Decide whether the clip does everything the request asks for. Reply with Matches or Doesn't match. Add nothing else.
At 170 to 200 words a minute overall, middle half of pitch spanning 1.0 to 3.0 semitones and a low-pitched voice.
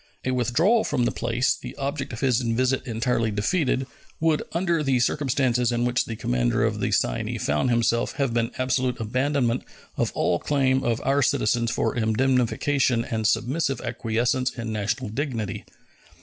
Doesn't match